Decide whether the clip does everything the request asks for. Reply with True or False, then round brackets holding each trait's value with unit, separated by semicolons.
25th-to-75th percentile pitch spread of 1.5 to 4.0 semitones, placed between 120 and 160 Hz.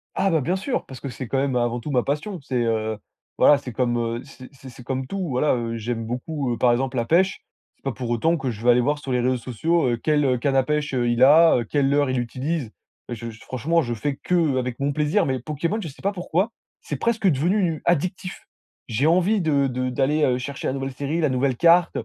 False (4.4 semitones; 135 Hz)